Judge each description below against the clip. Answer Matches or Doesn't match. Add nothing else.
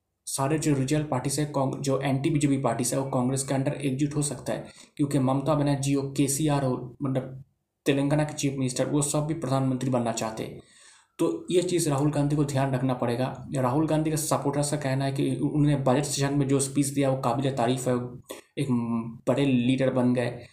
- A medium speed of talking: Doesn't match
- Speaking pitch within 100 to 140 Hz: Matches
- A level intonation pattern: Matches